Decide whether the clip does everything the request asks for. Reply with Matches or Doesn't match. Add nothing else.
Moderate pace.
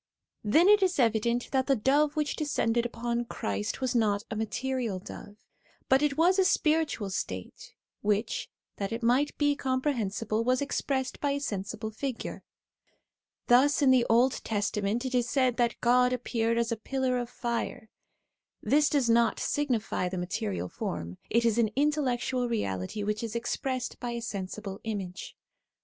Matches